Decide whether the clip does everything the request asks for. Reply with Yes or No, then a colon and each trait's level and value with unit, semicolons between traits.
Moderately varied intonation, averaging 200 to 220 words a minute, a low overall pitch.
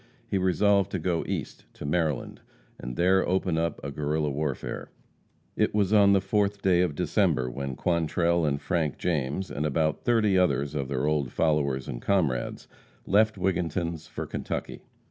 No: average, 4.8 semitones; average, 165 wpm; very low, 80 Hz